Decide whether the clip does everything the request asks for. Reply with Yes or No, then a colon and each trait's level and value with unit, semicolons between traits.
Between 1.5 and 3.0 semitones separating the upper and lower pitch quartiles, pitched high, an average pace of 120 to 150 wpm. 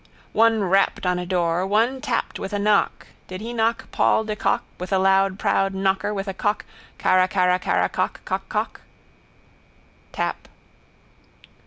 Yes: narrow, 2.4 semitones; high, 195 Hz; average, 145 wpm